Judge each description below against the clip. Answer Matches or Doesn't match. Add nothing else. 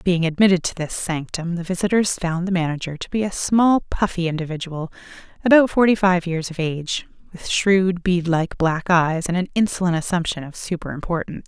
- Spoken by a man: Doesn't match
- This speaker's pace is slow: Doesn't match